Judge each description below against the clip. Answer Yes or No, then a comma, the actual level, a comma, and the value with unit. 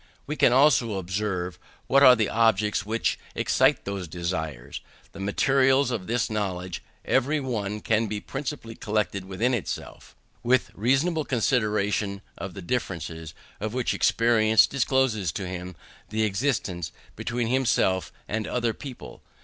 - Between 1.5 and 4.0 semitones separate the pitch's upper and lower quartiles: No, average, 4.6 semitones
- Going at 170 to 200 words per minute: No, slow, 135 wpm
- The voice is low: Yes, low, 110 Hz